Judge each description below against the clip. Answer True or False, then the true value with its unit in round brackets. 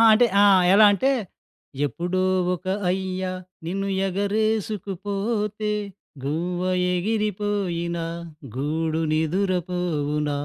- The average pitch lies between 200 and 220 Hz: False (185 Hz)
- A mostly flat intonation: False (3.3 semitones)